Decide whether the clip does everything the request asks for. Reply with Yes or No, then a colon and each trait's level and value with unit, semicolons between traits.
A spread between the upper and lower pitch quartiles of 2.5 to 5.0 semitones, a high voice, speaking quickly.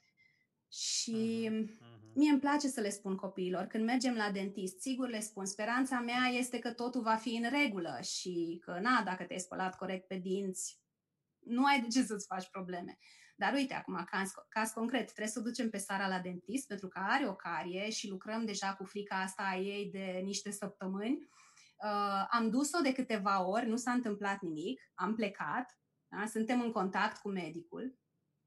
Yes: average, 4.1 semitones; high, 205 Hz; fast, 185 wpm